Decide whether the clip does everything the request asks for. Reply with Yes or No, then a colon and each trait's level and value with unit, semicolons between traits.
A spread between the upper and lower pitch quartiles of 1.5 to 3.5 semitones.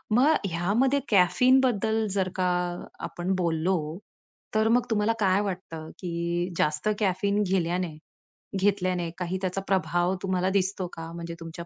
Yes: average, 2.9 semitones